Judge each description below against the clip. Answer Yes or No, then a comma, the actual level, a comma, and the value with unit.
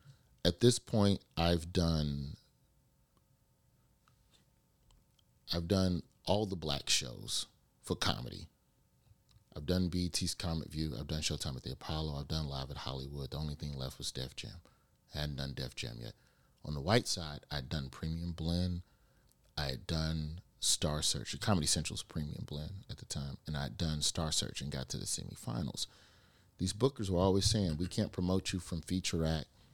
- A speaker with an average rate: Yes, average, 170 wpm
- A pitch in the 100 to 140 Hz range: No, very low, 80 Hz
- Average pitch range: Yes, average, 4.2 semitones